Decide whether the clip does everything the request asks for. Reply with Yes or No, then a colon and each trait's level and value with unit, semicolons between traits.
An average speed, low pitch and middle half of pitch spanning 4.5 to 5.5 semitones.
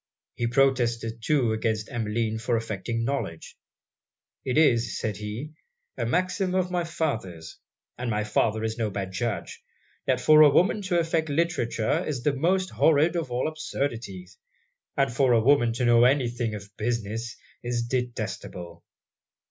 Yes: average, 155 wpm; low, 120 Hz; average, 4.8 semitones